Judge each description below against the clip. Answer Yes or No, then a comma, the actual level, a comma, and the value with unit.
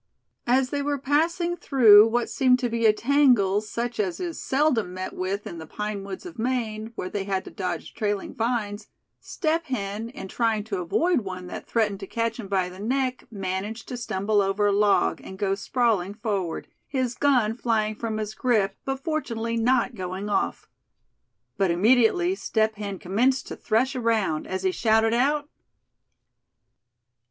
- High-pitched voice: Yes, high, 220 Hz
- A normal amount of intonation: Yes, average, 4.1 semitones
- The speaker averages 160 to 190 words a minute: Yes, average, 175 wpm